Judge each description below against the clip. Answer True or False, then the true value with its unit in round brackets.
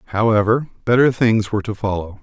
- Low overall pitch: True (110 Hz)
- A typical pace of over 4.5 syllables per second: True (6.1 syllables/s)